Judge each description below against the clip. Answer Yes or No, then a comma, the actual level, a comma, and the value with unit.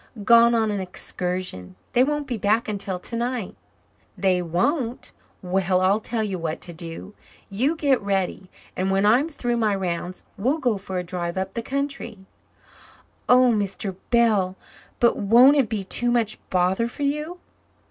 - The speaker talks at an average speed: Yes, average, 160 wpm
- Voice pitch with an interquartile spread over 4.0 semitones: Yes, average, 4.5 semitones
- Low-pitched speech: No, high, 210 Hz